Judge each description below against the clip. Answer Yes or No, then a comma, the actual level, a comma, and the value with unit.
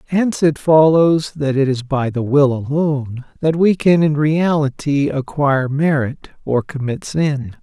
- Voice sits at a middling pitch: Yes, medium, 145 Hz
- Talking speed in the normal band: Yes, average, 155 wpm